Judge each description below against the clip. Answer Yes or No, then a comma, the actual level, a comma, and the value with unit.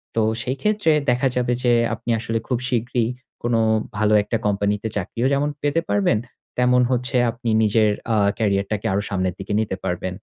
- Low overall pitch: Yes, low, 115 Hz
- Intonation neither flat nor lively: Yes, average, 3.4 semitones